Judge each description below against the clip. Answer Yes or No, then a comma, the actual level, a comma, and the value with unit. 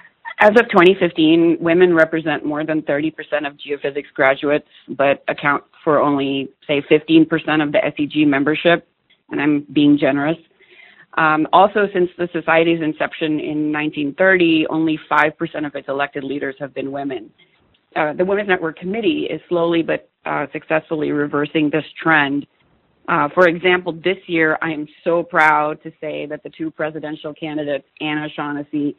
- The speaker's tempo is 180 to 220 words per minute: No, average, 150 wpm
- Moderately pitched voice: Yes, medium, 155 Hz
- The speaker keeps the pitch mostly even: Yes, narrow, 2.3 semitones